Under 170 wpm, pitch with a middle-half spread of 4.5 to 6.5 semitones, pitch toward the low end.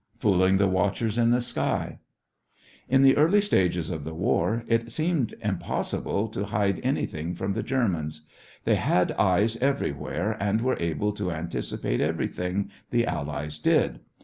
Yes: average, 145 wpm; average, 5.3 semitones; low, 100 Hz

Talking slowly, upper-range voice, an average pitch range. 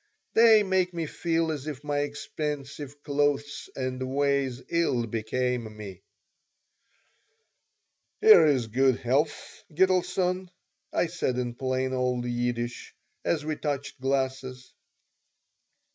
No: slow, 110 wpm; medium, 140 Hz; average, 3.6 semitones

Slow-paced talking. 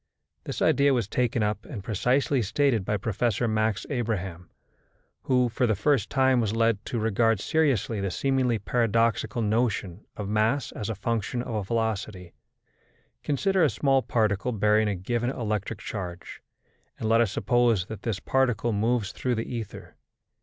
No: average, 155 wpm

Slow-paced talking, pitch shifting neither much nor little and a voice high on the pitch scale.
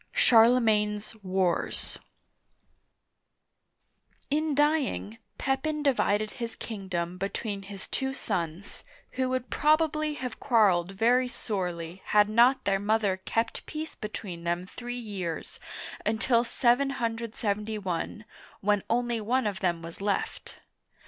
Yes: slow, 110 wpm; average, 4.3 semitones; high, 220 Hz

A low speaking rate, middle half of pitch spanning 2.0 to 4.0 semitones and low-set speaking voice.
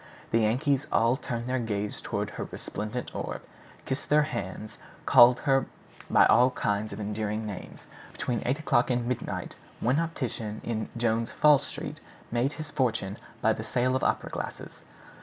No: average, 160 wpm; average, 3.3 semitones; low, 120 Hz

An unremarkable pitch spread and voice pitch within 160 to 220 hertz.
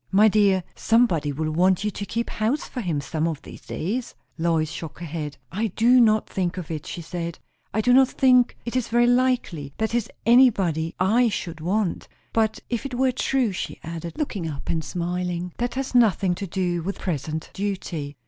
No: wide, 6.0 semitones; high, 190 Hz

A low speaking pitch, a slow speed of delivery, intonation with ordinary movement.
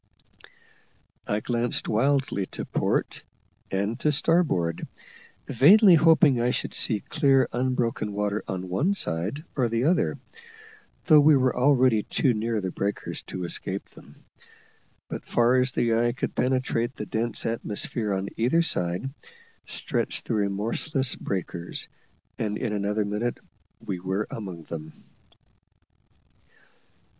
Yes: low, 115 Hz; slow, 130 wpm; average, 4.5 semitones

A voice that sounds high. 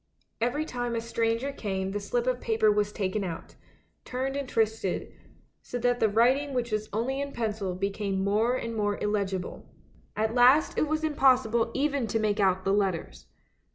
Yes: high, 225 Hz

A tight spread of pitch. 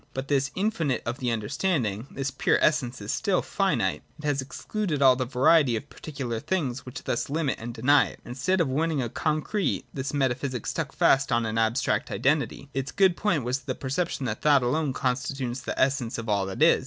No: average, 3.7 semitones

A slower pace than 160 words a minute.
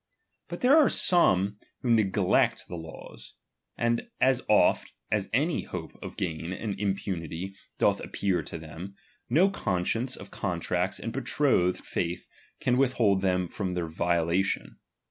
Yes: average, 140 wpm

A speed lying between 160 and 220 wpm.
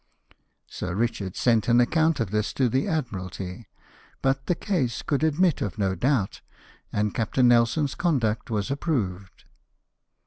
No: average, 145 wpm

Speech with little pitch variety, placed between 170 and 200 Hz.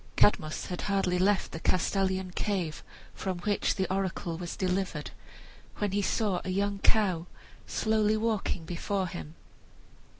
Yes: narrow, 2.3 semitones; high, 190 Hz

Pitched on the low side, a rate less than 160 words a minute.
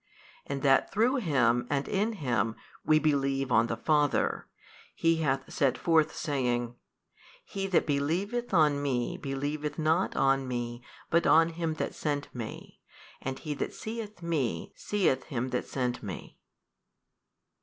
No: medium, 145 Hz; average, 145 wpm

